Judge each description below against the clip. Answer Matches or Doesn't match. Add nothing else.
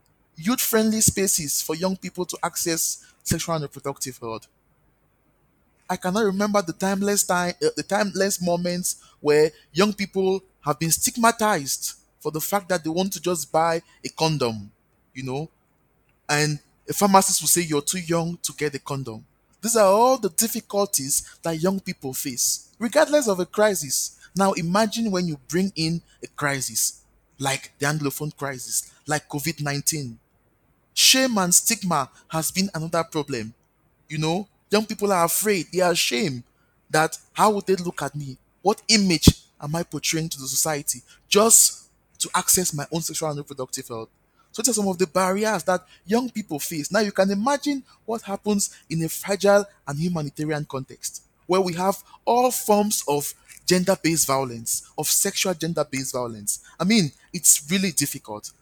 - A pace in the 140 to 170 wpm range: Matches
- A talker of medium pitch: Matches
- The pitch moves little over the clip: Doesn't match